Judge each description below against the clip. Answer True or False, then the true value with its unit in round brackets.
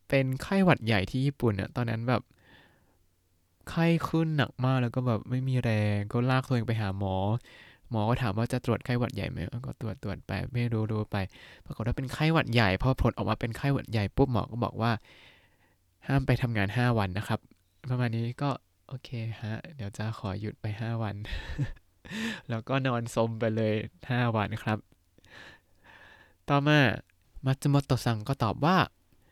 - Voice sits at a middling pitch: False (115 Hz)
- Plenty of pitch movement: False (3.8 semitones)